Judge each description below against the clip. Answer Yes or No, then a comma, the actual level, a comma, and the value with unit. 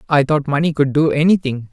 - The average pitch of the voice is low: No, medium, 145 Hz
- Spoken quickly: Yes, fast, 210 wpm